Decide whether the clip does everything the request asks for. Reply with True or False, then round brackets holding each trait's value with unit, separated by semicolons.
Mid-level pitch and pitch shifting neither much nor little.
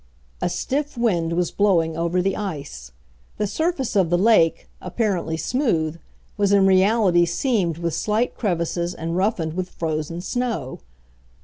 True (180 Hz; 4.2 semitones)